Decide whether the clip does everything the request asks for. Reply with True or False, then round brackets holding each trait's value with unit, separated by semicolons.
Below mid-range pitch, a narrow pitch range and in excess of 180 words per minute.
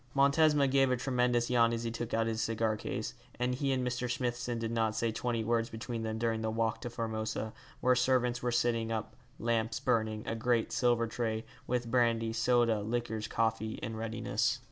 True (115 Hz; 1.6 semitones; 190 wpm)